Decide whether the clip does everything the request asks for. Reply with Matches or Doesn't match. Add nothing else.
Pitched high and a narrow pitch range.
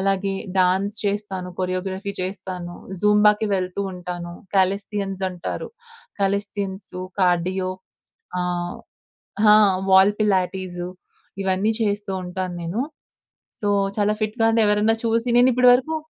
Matches